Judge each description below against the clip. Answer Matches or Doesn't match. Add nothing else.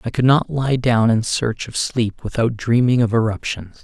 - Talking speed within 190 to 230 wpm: Matches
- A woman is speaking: Doesn't match